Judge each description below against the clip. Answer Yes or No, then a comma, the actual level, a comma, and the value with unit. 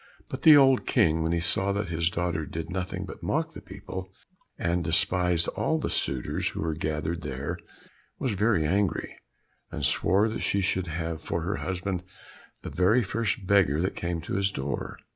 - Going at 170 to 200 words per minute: Yes, average, 180 wpm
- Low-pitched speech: Yes, very low, 90 Hz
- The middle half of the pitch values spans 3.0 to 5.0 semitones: Yes, average, 3.3 semitones